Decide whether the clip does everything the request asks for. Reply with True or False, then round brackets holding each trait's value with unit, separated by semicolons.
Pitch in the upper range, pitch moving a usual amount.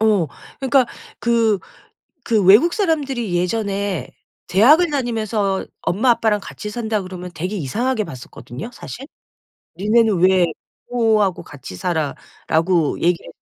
True (210 Hz; 4.6 semitones)